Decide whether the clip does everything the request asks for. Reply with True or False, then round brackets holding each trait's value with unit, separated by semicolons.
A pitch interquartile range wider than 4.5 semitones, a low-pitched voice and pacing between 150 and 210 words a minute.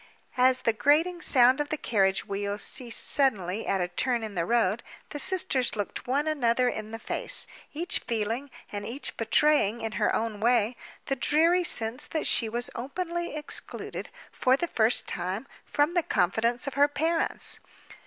False (5.1 semitones; 245 Hz; 170 wpm)